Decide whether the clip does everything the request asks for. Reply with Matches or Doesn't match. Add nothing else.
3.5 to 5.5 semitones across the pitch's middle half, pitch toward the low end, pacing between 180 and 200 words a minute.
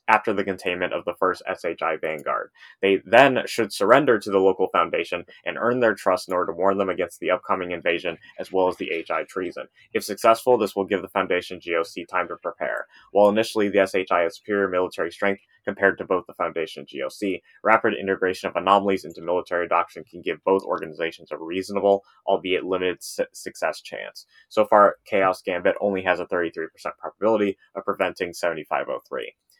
Doesn't match